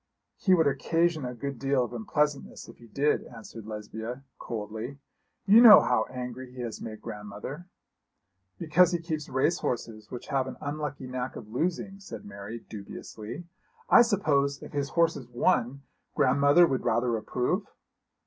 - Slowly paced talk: No, average, 155 wpm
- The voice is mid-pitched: No, low, 130 Hz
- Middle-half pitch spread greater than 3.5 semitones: Yes, average, 4.6 semitones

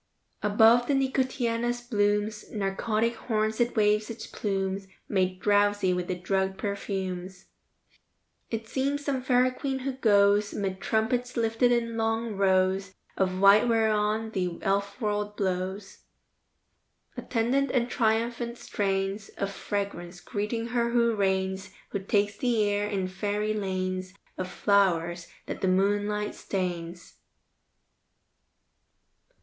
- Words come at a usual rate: No, slow, 120 wpm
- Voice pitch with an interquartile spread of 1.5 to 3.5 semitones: Yes, average, 3.0 semitones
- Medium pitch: No, high, 205 Hz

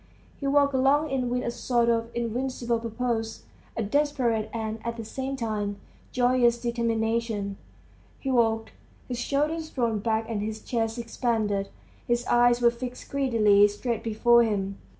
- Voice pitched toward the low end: No, high, 235 Hz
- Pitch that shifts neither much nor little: No, narrow, 2.1 semitones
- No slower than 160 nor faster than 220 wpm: No, average, 150 wpm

